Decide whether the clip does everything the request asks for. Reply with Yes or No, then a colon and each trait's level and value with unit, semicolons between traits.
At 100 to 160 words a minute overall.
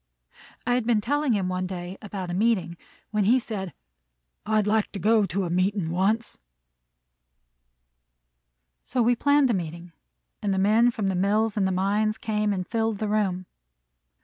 No: average, 170 wpm